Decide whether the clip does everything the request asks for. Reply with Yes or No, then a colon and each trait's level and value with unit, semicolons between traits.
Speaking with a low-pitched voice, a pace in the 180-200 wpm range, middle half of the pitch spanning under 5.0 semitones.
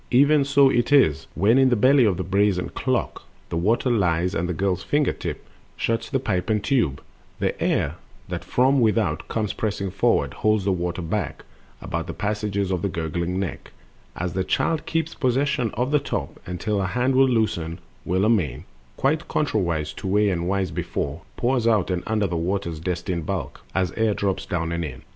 No: low, 100 Hz; average, 190 wpm; wide, 5.5 semitones